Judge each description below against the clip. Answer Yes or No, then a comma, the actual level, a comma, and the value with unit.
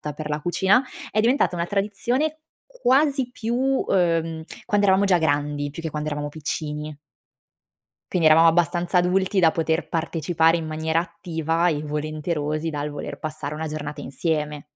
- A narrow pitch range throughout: No, average, 3.7 semitones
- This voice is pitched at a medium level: Yes, medium, 165 Hz